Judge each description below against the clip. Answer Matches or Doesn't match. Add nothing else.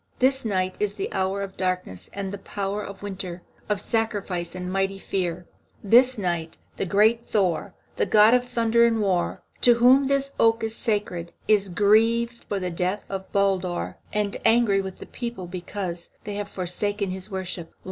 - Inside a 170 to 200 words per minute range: Matches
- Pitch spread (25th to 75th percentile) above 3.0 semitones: Matches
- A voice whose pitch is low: Doesn't match